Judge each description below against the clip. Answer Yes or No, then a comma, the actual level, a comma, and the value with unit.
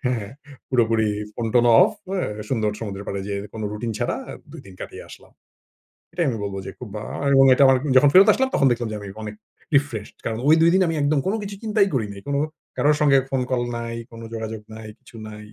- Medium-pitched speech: No, low, 120 Hz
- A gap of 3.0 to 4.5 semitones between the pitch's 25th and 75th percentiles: No, average, 4.9 semitones